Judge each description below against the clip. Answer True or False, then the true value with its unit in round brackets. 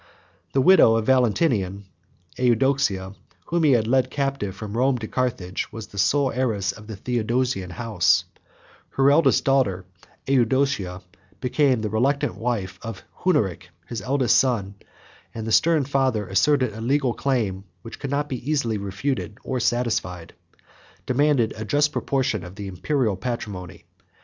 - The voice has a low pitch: True (120 Hz)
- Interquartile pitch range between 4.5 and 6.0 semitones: True (4.9 semitones)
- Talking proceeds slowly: False (145 wpm)